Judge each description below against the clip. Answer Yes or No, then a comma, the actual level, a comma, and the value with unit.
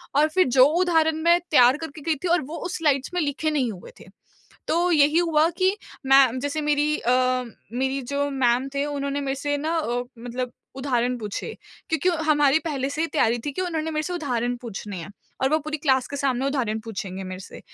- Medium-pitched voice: No, very high, 280 Hz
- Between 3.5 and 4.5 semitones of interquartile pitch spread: Yes, average, 3.8 semitones